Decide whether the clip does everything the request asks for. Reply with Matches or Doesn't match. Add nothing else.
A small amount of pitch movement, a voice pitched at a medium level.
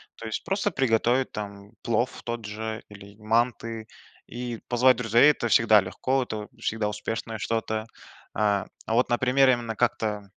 Doesn't match